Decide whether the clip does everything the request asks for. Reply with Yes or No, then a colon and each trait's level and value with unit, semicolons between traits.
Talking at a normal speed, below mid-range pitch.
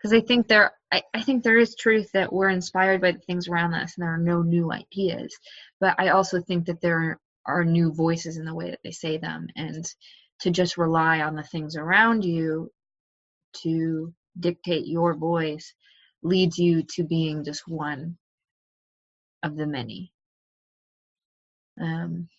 No: average, 170 wpm; medium, 170 Hz